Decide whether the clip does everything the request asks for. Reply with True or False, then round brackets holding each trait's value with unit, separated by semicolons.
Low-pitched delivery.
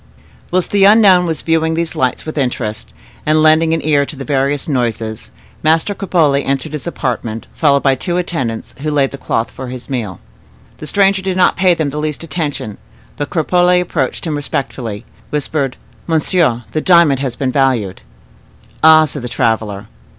False (145 Hz)